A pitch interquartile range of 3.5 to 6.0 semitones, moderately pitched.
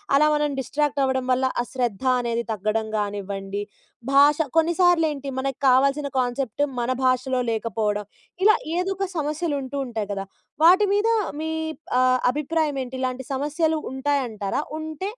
No: average, 4.2 semitones; very high, 265 Hz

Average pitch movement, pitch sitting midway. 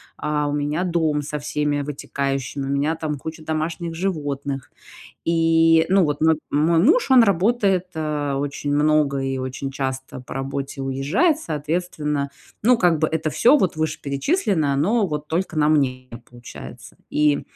Yes: average, 3.0 semitones; medium, 150 Hz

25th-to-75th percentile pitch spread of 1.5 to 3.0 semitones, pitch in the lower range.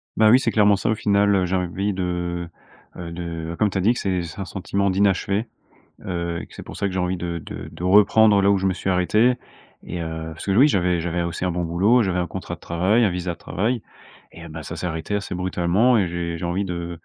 Yes: average, 2.7 semitones; very low, 90 Hz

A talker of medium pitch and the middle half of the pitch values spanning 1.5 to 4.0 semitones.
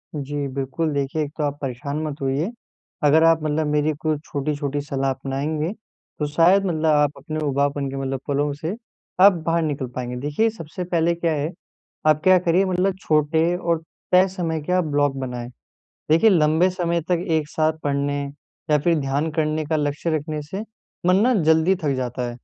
Yes: medium, 155 Hz; average, 2.8 semitones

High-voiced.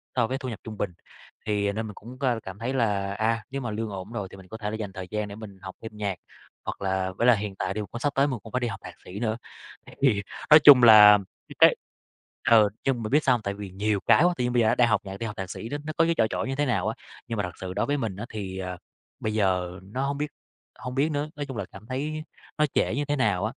No: low, 110 Hz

